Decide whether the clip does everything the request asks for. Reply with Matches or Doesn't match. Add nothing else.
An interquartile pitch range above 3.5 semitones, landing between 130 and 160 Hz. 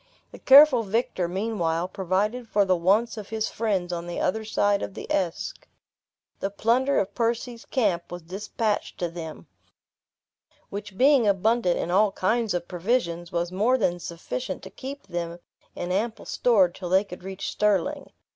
Doesn't match